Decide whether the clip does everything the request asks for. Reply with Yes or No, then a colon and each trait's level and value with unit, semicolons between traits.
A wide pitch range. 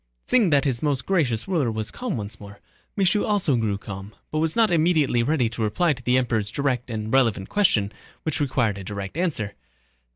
Yes: wide, 6.8 semitones